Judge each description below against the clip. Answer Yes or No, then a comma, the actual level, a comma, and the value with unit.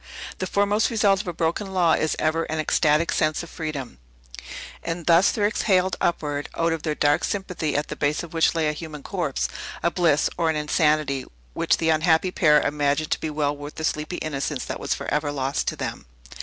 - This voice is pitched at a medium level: Yes, medium, 155 Hz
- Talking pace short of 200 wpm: No, fast, 205 wpm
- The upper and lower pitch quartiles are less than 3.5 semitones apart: Yes, narrow, 2.5 semitones